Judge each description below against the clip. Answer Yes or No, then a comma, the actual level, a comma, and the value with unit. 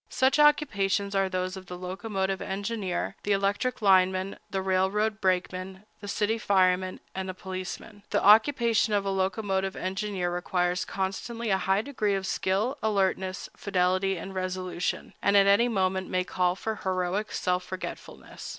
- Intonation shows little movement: Yes, narrow, 1.8 semitones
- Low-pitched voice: No, high, 190 Hz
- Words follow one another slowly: No, average, 150 wpm